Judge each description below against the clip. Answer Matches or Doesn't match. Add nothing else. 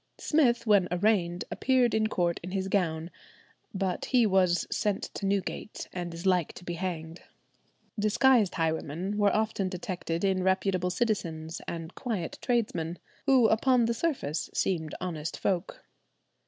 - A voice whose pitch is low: Doesn't match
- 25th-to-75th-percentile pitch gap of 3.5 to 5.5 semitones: Matches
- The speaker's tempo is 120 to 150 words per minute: Matches